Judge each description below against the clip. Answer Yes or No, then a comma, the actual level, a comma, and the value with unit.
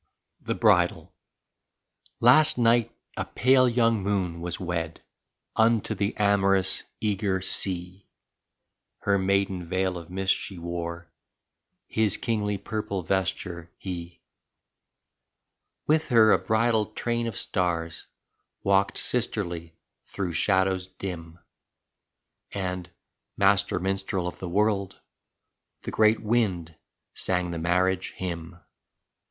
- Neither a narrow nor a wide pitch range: Yes, average, 3.3 semitones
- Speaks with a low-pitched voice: Yes, very low, 95 Hz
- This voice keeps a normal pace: No, slow, 110 wpm